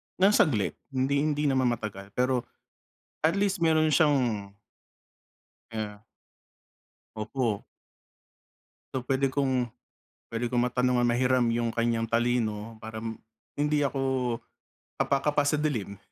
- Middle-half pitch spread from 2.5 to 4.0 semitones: Yes, average, 3.7 semitones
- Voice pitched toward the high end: No, low, 125 Hz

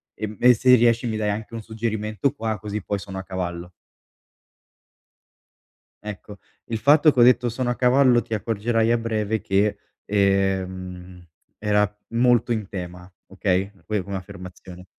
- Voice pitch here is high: No, low, 105 Hz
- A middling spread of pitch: Yes, average, 3.3 semitones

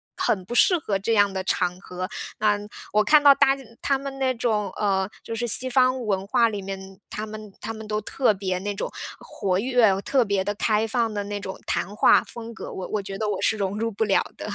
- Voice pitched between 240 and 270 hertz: No, high, 210 Hz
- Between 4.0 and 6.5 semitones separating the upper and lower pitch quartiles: No, average, 3.2 semitones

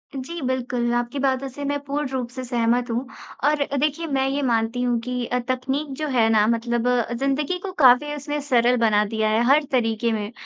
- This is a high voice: Yes, very high, 250 Hz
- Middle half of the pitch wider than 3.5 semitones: No, average, 3.0 semitones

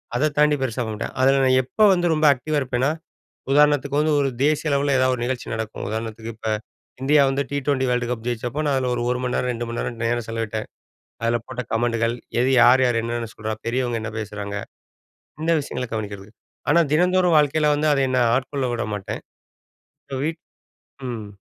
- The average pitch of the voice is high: No, low, 125 Hz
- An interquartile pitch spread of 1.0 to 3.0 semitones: No, average, 3.7 semitones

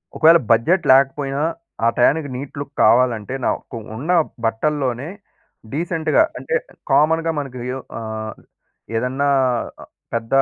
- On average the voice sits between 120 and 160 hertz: Yes, low, 135 Hz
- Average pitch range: Yes, average, 4.2 semitones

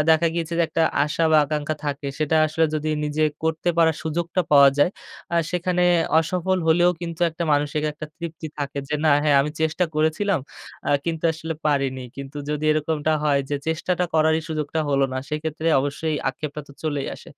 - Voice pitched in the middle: Yes, medium, 155 Hz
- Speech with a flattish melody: Yes, narrow, 1.8 semitones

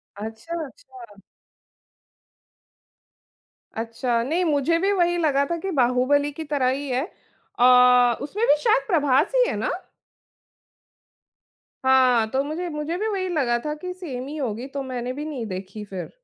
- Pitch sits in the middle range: No, very high, 280 Hz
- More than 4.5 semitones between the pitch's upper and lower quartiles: Yes, average, 5.2 semitones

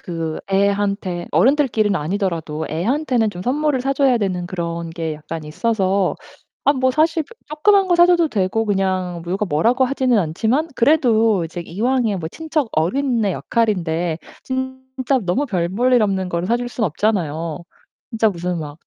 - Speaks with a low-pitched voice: No, high, 205 Hz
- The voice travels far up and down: Yes, wide, 7.0 semitones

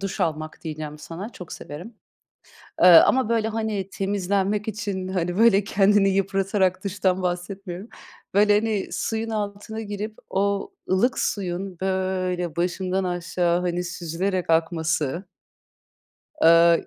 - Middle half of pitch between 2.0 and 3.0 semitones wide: Yes, narrow, 2.6 semitones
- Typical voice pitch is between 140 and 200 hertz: Yes, high, 190 Hz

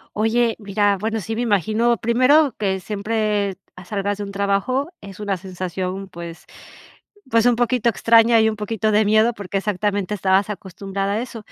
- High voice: Yes, high, 210 Hz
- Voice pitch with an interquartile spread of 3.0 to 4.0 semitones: No, narrow, 2.5 semitones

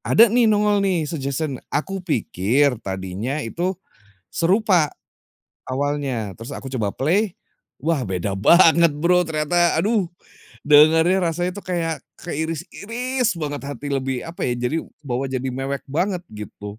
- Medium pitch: Yes, medium, 155 Hz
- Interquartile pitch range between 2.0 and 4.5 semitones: No, average, 5.1 semitones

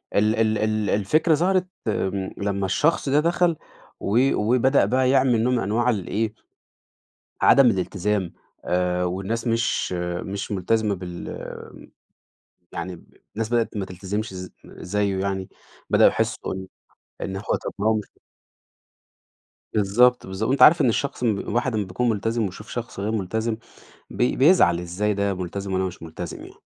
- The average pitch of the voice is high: No, low, 105 Hz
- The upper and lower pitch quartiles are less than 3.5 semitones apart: No, average, 4.0 semitones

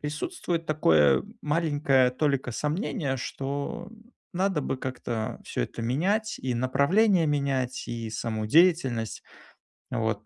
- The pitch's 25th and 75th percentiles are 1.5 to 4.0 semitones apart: No, average, 5.3 semitones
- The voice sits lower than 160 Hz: Yes, medium, 140 Hz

